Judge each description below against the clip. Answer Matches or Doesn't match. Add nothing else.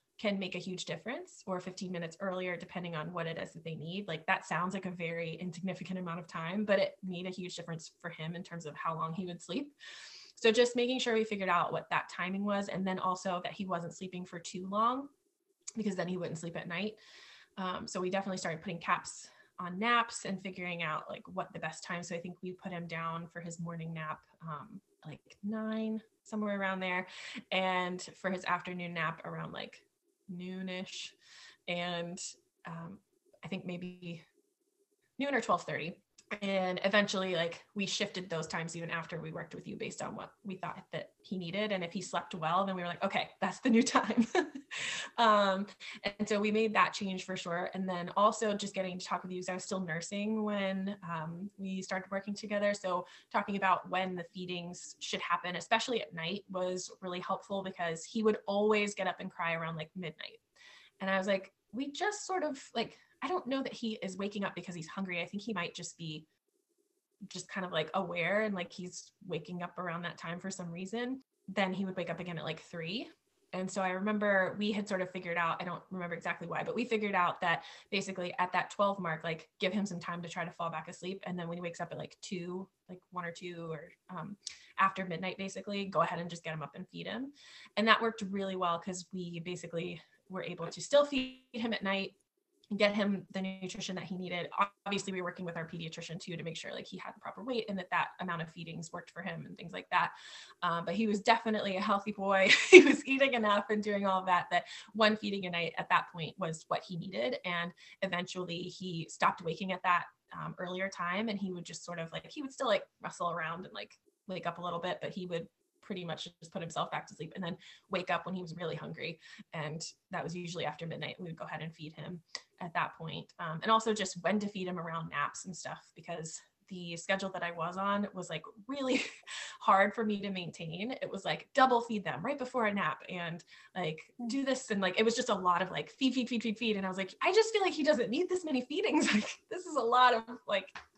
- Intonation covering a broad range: Doesn't match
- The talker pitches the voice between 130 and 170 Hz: Doesn't match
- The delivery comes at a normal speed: Doesn't match